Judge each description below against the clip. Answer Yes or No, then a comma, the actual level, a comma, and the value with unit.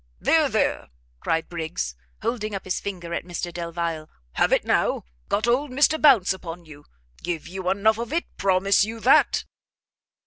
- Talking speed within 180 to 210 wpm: No, average, 165 wpm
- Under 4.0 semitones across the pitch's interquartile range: No, average, 4.5 semitones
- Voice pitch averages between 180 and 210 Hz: Yes, medium, 185 Hz